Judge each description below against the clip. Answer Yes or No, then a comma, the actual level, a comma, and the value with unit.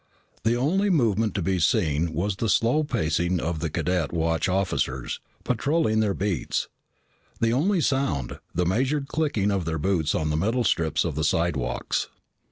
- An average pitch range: No, wide, 6.9 semitones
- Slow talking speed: No, average, 165 wpm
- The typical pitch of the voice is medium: No, very low, 95 Hz